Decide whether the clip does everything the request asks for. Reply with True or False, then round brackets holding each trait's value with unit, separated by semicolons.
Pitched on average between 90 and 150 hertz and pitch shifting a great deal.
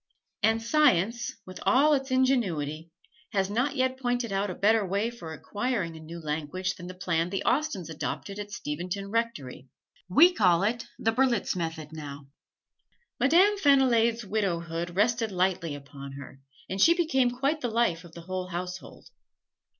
False (200 Hz; 6.3 semitones)